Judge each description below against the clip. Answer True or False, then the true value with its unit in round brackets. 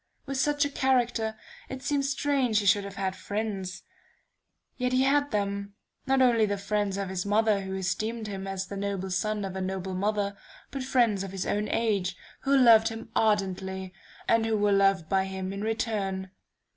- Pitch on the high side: True (205 Hz)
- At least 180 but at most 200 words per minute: True (185 wpm)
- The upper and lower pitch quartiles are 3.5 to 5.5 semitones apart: False (3.1 semitones)